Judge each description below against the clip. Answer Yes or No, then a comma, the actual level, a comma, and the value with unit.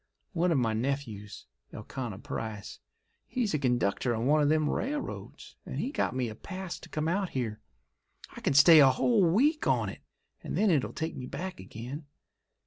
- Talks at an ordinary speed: Yes, average, 185 wpm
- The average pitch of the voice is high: No, medium, 145 Hz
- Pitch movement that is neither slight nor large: No, wide, 6.9 semitones